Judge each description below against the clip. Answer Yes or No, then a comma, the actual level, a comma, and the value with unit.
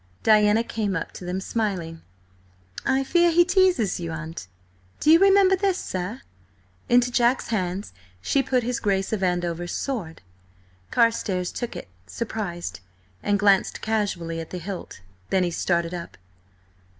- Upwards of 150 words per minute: No, average, 145 wpm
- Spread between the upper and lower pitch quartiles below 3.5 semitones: No, wide, 5.6 semitones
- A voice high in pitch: Yes, high, 205 Hz